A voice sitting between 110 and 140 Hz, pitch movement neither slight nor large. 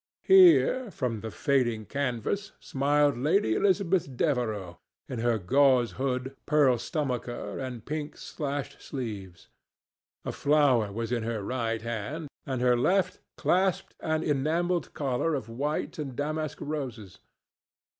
Yes: low, 135 Hz; average, 4.5 semitones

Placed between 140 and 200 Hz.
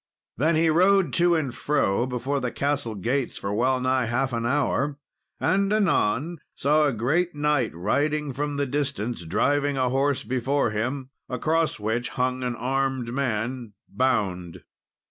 No: low, 130 Hz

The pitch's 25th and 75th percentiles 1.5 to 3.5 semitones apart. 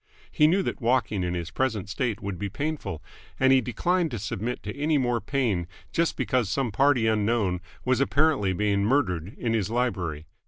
No: average, 5.0 semitones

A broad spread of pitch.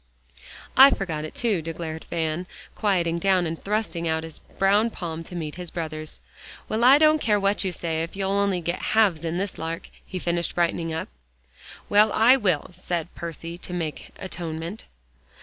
No: average, 3.4 semitones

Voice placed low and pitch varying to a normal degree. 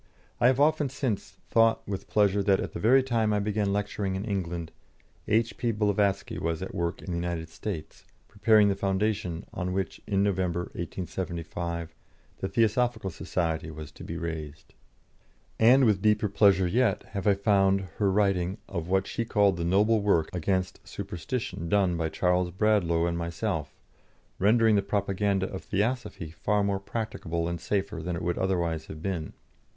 Yes: very low, 95 Hz; average, 3.4 semitones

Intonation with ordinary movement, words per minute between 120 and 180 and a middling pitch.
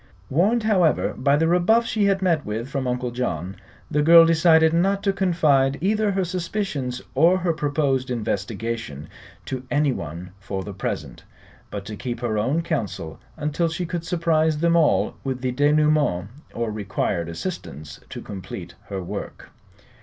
No: wide, 7.7 semitones; average, 155 wpm; medium, 145 Hz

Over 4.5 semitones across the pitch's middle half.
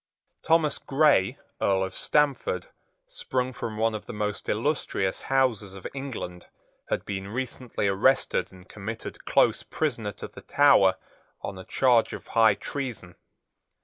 Yes: wide, 5.5 semitones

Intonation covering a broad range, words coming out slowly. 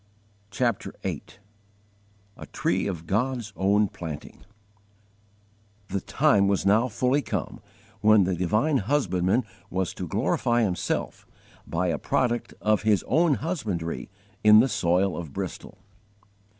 No: average, 4.6 semitones; slow, 125 wpm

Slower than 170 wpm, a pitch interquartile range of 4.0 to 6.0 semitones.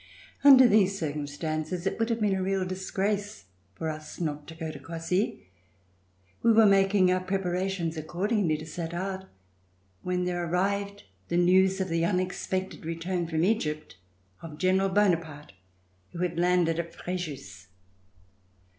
No: average, 145 wpm; average, 2.9 semitones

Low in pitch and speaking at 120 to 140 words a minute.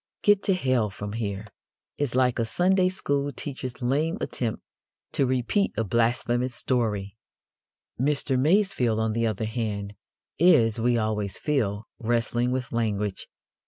Yes: low, 120 Hz; slow, 135 wpm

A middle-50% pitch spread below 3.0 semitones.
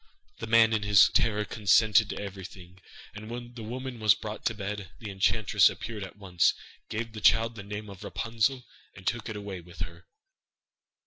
Yes: narrow, 2.6 semitones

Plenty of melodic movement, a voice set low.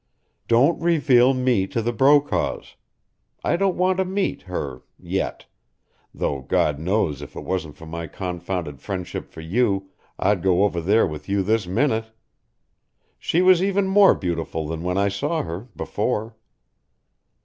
Yes: wide, 7.6 semitones; low, 100 Hz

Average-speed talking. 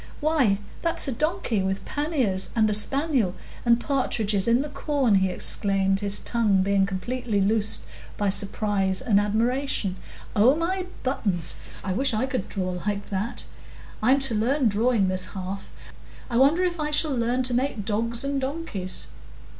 Yes: average, 160 wpm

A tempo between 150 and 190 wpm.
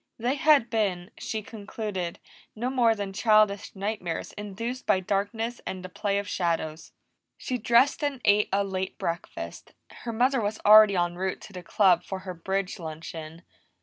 Yes: average, 165 wpm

